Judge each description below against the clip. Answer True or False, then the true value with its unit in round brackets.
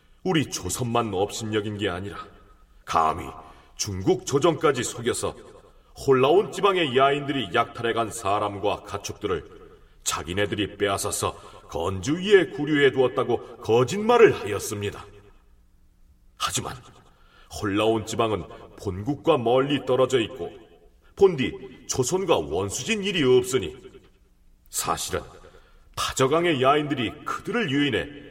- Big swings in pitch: True (6.3 semitones)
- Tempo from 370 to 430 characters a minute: False (260 characters per minute)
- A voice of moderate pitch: False (130 Hz)